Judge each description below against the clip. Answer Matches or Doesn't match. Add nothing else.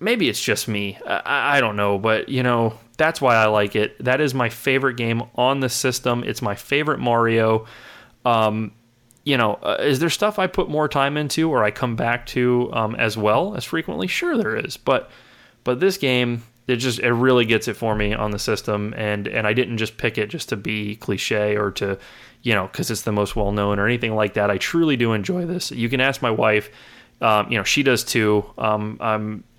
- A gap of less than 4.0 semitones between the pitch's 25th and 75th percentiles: Matches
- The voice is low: Matches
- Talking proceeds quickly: Matches